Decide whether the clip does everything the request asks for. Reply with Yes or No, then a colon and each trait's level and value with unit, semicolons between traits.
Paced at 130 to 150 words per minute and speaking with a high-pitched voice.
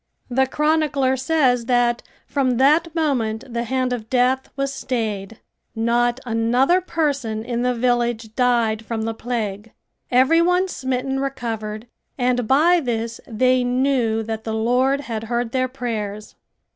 Yes: average, 140 wpm; high, 245 Hz